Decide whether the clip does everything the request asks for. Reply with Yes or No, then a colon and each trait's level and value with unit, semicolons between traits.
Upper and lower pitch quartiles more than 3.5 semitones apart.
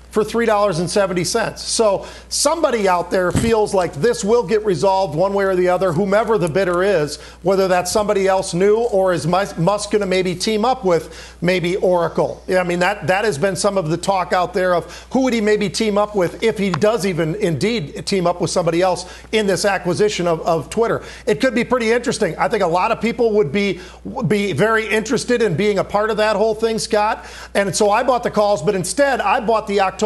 No: average, 3.1 semitones